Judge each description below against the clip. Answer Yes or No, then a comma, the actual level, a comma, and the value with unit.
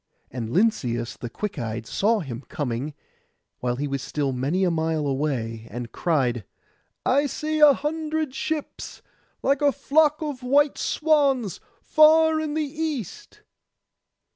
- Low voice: No, high, 210 Hz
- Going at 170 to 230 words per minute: No, average, 140 wpm